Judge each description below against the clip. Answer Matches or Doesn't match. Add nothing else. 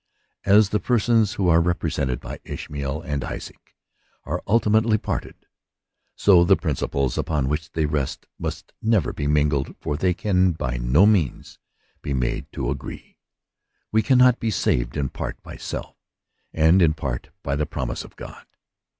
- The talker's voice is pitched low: Matches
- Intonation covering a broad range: Matches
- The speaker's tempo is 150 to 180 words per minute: Matches